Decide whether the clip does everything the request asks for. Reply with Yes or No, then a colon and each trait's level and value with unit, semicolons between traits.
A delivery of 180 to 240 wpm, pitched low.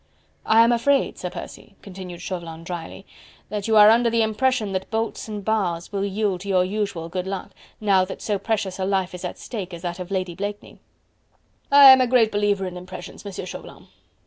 No: average, 200 wpm; high, 195 Hz